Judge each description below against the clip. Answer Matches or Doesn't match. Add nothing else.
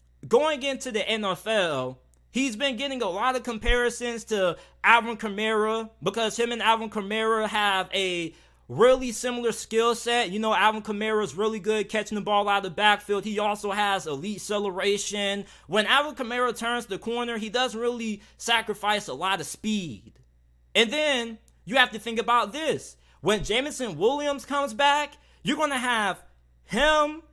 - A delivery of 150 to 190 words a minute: Matches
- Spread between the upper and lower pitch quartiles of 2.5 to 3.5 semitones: Matches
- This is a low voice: Doesn't match